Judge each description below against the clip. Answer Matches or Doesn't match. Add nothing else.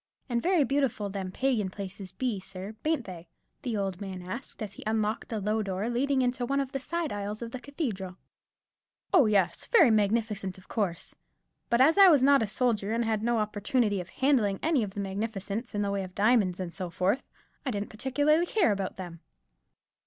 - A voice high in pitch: Matches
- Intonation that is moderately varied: Matches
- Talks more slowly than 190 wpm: Doesn't match